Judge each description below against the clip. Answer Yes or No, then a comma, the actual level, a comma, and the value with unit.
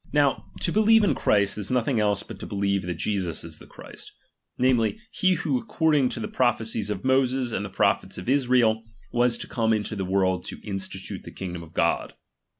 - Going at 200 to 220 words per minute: Yes, fast, 205 wpm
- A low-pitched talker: Yes, low, 110 Hz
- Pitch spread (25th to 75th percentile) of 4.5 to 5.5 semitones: Yes, average, 4.9 semitones